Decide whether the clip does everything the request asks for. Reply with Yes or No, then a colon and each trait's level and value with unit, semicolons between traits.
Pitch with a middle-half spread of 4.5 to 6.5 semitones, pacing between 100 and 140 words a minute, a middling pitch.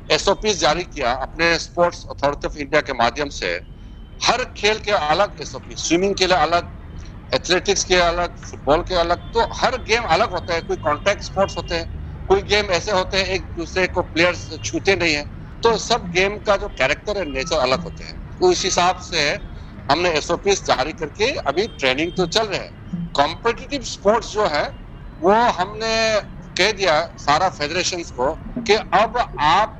No: average, 4.9 semitones; average, 165 wpm; medium, 175 Hz